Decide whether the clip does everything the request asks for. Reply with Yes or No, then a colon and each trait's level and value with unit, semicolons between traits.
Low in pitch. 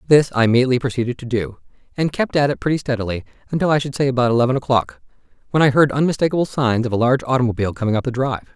Yes: low, 125 Hz